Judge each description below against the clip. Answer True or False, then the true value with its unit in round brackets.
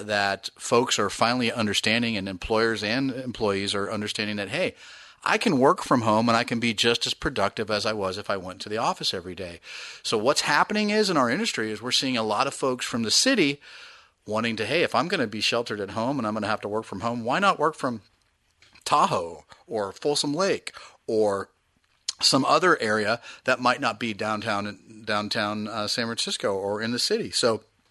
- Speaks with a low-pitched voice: True (110 Hz)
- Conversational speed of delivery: False (215 wpm)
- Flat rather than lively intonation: False (3.2 semitones)